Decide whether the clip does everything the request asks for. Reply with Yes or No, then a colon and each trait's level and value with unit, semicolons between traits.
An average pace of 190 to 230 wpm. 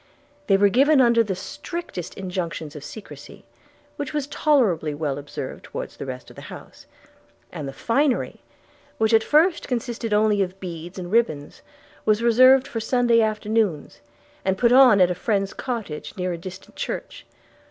No: average, 165 wpm